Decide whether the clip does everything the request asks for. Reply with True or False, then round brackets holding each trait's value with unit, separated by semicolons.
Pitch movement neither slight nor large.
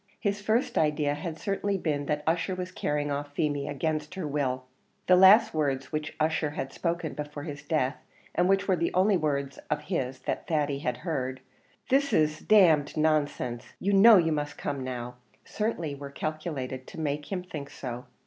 True (4.0 semitones)